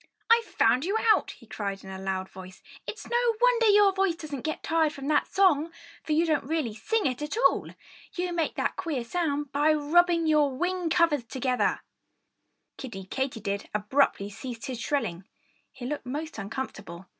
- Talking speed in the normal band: Yes, average, 175 wpm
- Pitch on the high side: Yes, very high, 290 Hz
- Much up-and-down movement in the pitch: Yes, wide, 6.4 semitones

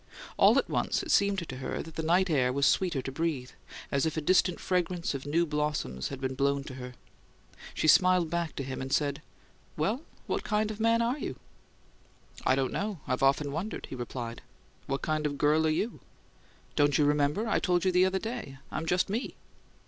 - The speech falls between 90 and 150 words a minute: No, fast, 205 wpm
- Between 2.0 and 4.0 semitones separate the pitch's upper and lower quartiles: No, average, 5.0 semitones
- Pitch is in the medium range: Yes, medium, 155 Hz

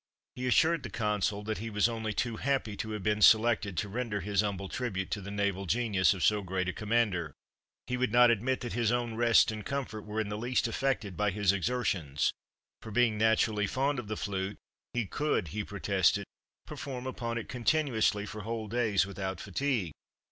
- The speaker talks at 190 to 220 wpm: Yes, average, 195 wpm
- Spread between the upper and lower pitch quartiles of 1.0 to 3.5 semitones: Yes, average, 3.0 semitones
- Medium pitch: No, low, 110 Hz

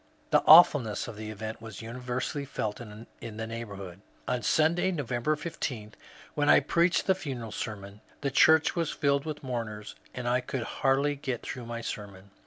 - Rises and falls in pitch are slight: No, average, 5.1 semitones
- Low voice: Yes, low, 120 Hz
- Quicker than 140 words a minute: Yes, average, 170 wpm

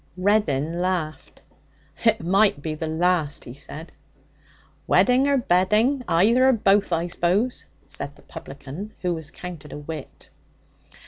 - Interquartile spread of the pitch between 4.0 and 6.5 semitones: Yes, average, 5.2 semitones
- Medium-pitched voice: Yes, medium, 180 Hz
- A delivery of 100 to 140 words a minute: Yes, slow, 135 wpm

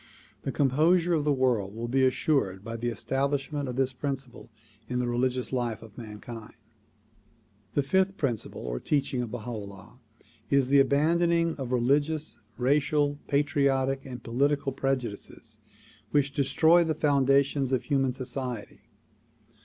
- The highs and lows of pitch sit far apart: No, average, 2.9 semitones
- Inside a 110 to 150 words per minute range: Yes, average, 140 wpm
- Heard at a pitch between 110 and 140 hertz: Yes, low, 135 Hz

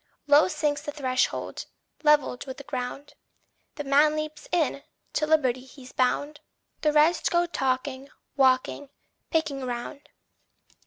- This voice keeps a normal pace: No, slow, 125 wpm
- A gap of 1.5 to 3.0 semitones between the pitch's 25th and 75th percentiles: Yes, narrow, 2.6 semitones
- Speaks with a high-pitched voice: Yes, very high, 285 Hz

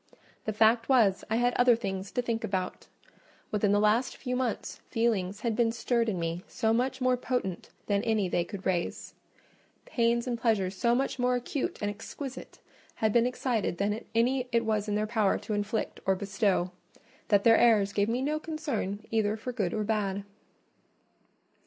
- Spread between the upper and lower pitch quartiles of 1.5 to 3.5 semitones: Yes, average, 3.1 semitones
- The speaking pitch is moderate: No, high, 220 Hz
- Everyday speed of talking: Yes, average, 175 wpm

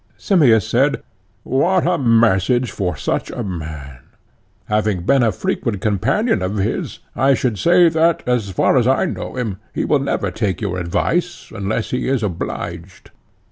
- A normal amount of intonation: No, wide, 6.3 semitones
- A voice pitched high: No, low, 115 Hz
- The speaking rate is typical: Yes, average, 160 wpm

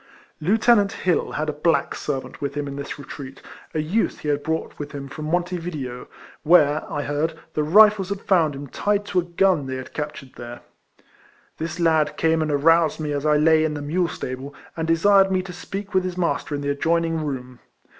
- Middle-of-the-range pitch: Yes, medium, 155 Hz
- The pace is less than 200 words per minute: No, fast, 205 wpm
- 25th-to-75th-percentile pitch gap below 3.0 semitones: No, average, 3.6 semitones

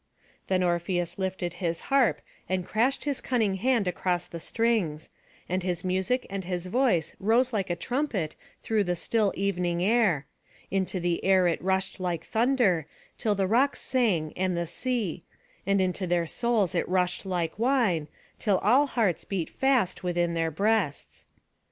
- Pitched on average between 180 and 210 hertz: Yes, high, 190 Hz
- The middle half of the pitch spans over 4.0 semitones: Yes, average, 4.4 semitones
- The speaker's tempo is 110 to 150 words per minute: No, average, 160 wpm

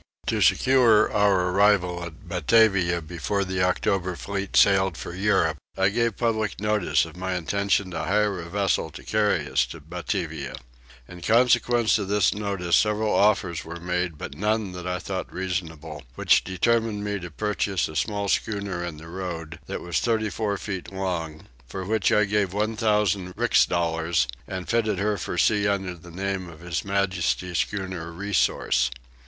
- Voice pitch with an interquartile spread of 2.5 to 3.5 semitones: Yes, average, 3.1 semitones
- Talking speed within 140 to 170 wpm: Yes, average, 165 wpm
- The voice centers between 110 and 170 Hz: No, very low, 95 Hz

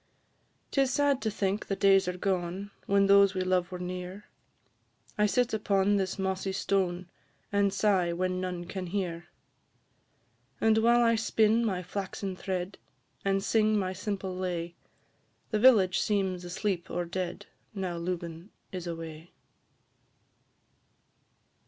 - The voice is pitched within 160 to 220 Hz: Yes, high, 190 Hz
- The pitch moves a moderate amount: No, narrow, 2.2 semitones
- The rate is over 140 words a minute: No, slow, 135 wpm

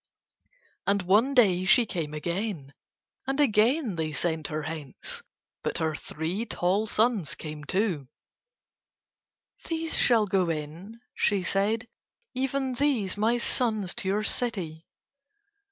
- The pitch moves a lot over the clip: Yes, wide, 6.2 semitones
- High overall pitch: Yes, high, 200 Hz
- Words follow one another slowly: Yes, slow, 120 wpm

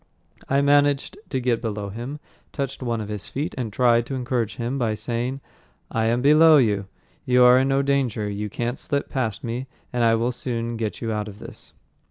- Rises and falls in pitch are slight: No, average, 3.1 semitones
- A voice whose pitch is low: Yes, low, 120 Hz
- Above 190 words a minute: Yes, fast, 205 wpm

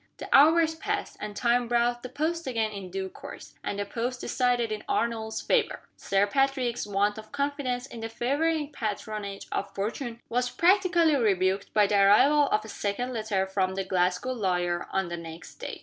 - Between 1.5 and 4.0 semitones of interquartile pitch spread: No, average, 5.0 semitones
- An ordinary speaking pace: Yes, average, 180 wpm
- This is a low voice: No, high, 230 Hz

